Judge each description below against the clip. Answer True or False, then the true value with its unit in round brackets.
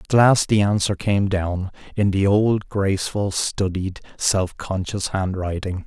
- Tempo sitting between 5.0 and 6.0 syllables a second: False (4.0 syllables/s)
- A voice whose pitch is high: False (100 Hz)